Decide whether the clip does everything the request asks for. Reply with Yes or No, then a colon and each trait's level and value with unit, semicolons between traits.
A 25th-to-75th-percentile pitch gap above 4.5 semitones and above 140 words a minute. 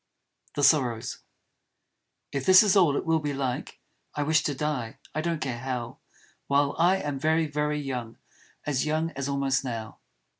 No: average, 2.9 semitones; average, 165 wpm